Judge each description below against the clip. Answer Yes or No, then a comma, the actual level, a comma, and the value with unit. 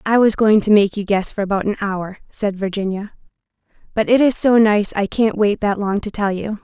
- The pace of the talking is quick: Yes, fast, 235 wpm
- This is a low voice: No, high, 205 Hz